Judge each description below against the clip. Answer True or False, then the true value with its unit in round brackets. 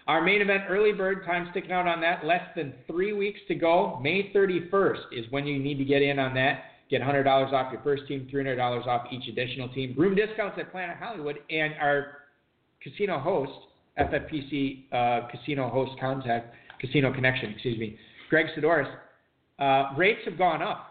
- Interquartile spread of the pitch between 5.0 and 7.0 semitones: True (5.3 semitones)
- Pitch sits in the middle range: True (145 Hz)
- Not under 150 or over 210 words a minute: True (180 wpm)